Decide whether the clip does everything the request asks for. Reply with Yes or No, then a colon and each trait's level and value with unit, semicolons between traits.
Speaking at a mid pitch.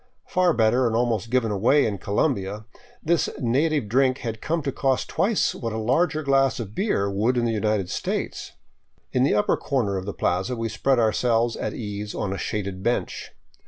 No: low, 115 Hz